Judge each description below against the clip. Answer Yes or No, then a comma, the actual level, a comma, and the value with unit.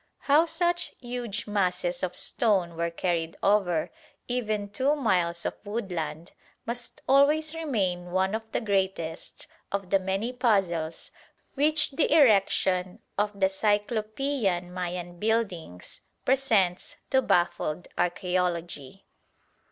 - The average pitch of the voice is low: No, high, 195 Hz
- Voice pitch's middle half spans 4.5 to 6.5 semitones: Yes, average, 5.2 semitones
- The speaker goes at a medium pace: No, slow, 115 wpm